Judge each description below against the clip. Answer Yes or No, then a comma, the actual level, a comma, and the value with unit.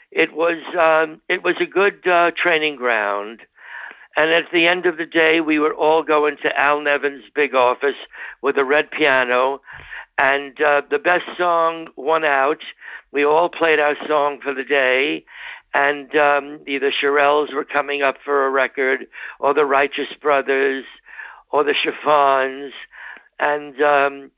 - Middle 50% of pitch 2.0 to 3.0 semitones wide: Yes, narrow, 2.6 semitones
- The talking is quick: No, average, 160 wpm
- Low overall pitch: No, medium, 145 Hz